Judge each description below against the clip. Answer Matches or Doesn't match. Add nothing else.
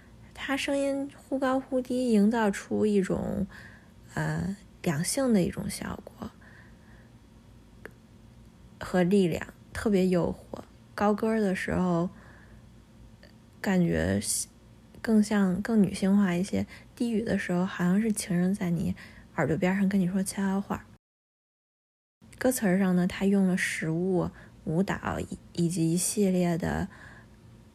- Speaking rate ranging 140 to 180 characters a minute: Matches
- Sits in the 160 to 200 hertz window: Matches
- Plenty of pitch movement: Doesn't match